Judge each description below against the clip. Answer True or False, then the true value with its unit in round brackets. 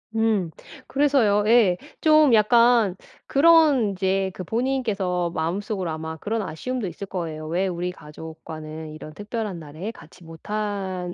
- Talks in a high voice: True (195 Hz)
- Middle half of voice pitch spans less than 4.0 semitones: False (5.1 semitones)